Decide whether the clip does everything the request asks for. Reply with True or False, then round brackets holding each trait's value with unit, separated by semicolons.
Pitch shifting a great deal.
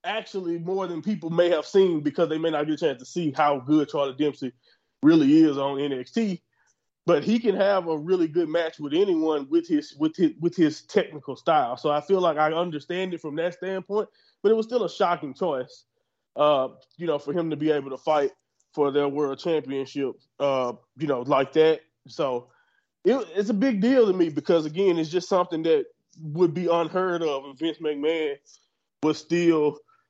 True (6.0 semitones)